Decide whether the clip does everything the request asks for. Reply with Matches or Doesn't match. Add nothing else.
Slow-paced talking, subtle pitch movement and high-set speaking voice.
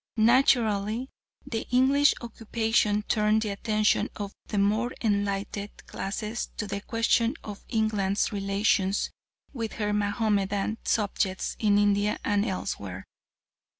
Matches